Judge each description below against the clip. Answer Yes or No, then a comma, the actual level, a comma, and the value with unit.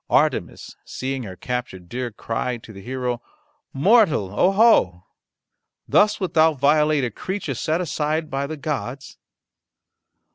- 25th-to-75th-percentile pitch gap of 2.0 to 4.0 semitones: No, average, 4.6 semitones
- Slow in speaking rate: Yes, slow, 130 wpm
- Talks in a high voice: No, low, 135 Hz